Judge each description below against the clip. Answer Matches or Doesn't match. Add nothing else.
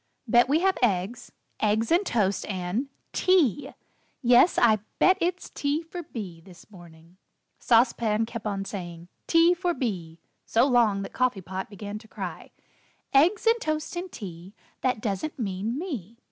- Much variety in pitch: Matches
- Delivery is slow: Doesn't match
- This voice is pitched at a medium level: Doesn't match